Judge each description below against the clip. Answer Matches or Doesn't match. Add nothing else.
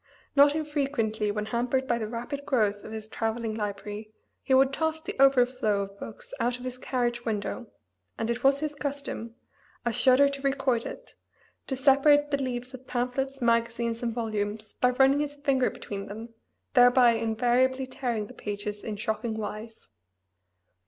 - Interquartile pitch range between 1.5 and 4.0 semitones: Matches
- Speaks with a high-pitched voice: Matches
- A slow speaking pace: Doesn't match